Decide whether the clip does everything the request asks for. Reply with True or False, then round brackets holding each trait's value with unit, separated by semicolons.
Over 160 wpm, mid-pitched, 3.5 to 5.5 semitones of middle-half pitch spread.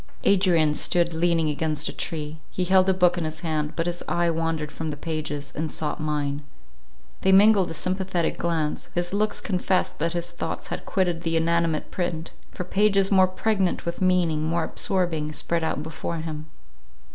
False (180 wpm; 170 Hz; 2.7 semitones)